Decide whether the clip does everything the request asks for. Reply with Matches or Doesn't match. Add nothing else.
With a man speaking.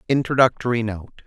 Matches